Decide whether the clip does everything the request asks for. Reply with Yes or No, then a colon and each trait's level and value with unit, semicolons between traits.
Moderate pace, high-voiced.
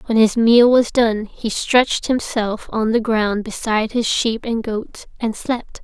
Yes: average, 185 wpm; high, 225 Hz